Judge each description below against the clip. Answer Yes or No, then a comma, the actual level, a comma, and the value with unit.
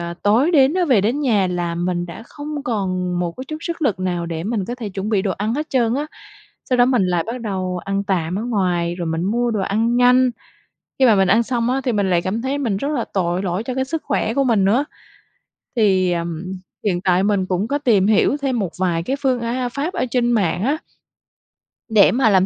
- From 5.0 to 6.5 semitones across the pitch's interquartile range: Yes, wide, 5.4 semitones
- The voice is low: No, high, 215 Hz